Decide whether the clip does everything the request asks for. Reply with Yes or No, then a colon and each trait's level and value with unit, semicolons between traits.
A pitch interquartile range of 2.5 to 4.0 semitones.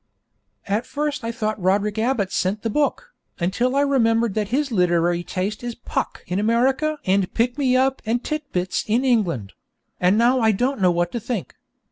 No: average, 5.1 semitones